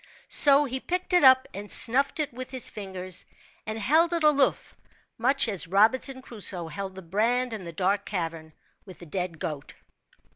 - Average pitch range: No, wide, 6.1 semitones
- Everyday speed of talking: Yes, average, 175 wpm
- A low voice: No, high, 215 Hz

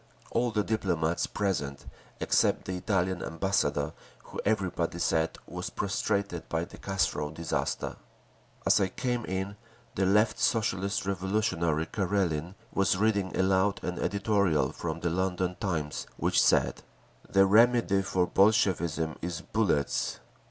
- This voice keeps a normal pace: No, slow, 125 wpm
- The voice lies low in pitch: Yes, very low, 95 Hz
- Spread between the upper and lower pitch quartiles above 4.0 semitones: No, average, 2.9 semitones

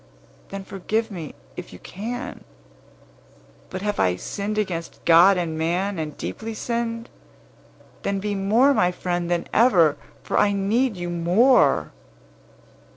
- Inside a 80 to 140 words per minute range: Yes, slow, 135 wpm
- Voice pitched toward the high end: Yes, high, 195 Hz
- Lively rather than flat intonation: No, average, 4.2 semitones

